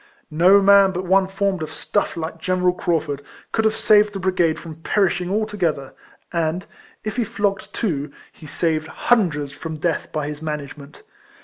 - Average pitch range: Yes, average, 4.1 semitones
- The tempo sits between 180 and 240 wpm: No, average, 165 wpm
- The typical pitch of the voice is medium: Yes, medium, 175 Hz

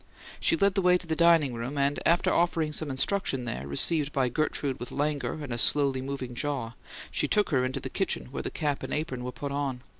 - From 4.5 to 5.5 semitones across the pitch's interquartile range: No, average, 3.7 semitones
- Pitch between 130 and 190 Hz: Yes, medium, 140 Hz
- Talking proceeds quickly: Yes, fast, 230 wpm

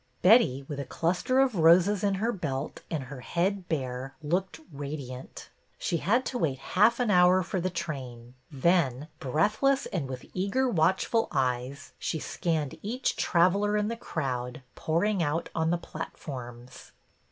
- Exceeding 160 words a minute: No, average, 155 wpm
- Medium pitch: Yes, medium, 165 Hz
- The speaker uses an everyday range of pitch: No, wide, 6.4 semitones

